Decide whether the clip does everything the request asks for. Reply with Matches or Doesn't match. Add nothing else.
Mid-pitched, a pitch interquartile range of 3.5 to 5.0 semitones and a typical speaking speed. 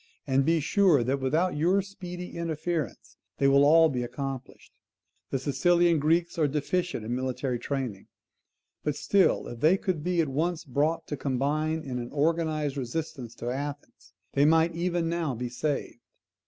Matches